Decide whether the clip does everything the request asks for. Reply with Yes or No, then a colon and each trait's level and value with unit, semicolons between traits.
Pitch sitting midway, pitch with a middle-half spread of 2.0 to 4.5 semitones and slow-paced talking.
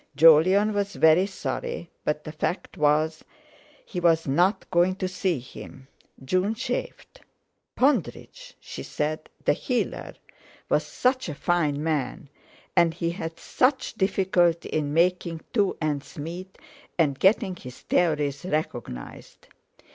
Yes: medium, 170 Hz; average, 3.9 semitones; slow, 120 wpm